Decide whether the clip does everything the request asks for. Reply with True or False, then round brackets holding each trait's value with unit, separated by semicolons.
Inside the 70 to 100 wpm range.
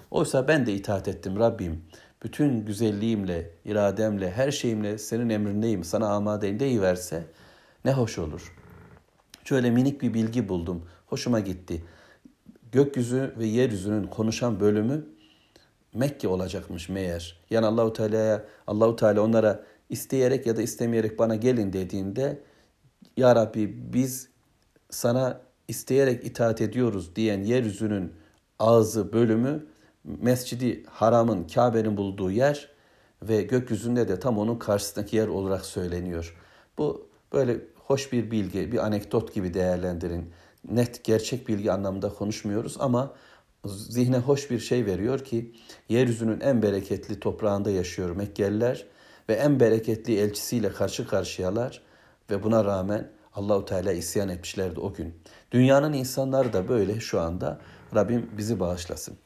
False (125 wpm)